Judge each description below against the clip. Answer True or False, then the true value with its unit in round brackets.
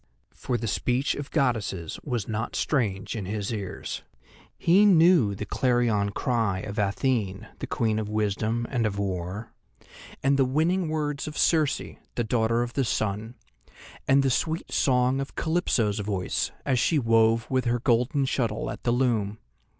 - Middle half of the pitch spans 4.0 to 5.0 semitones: True (4.3 semitones)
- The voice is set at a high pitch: False (120 Hz)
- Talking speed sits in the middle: True (160 wpm)